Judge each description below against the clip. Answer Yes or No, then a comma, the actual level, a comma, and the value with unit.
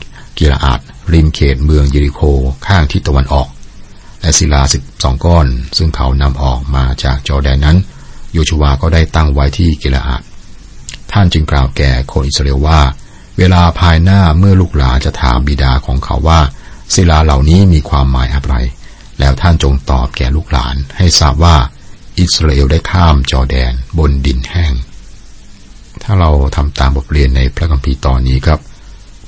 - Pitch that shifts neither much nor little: Yes, average, 3.9 semitones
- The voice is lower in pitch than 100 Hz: Yes, very low, 75 Hz